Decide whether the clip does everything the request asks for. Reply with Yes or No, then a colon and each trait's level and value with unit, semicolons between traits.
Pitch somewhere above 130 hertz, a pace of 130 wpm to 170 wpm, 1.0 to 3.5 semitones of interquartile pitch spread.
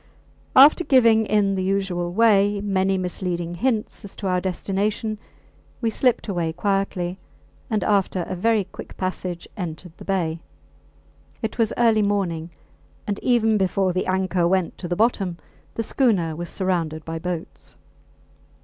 Yes: high, 190 Hz; average, 145 wpm; average, 3.2 semitones